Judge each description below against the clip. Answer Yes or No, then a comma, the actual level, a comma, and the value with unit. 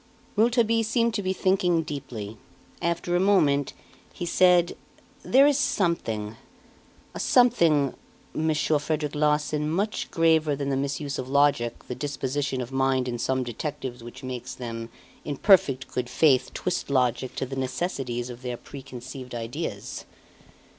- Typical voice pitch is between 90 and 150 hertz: Yes, medium, 140 Hz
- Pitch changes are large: No, average, 5.0 semitones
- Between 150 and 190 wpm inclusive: No, average, 140 wpm